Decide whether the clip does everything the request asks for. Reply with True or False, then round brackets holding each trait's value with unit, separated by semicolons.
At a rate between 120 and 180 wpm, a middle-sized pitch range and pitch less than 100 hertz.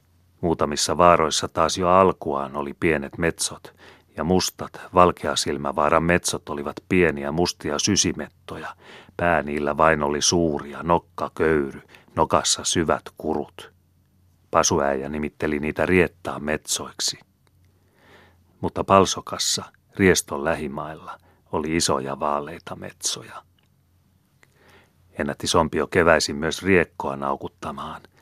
False (95 wpm; 3.6 semitones; 80 Hz)